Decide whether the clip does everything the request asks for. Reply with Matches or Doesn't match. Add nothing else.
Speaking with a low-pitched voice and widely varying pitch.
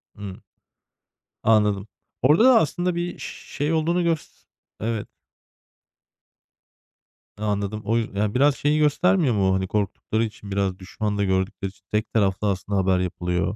Matches